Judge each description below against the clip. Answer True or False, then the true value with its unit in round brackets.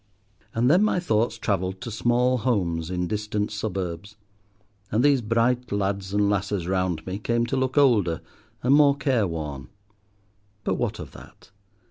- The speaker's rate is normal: True (150 wpm)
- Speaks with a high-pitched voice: False (105 Hz)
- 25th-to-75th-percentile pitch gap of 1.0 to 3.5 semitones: False (4.8 semitones)